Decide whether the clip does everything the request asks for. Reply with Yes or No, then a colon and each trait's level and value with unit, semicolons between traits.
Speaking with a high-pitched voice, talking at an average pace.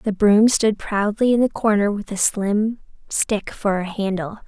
Yes: high, 210 Hz; average, 190 wpm